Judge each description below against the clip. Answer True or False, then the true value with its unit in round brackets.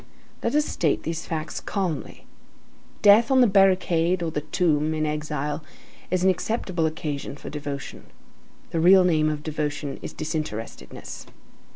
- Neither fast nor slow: True (145 wpm)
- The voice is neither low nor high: True (160 Hz)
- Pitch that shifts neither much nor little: True (3.5 semitones)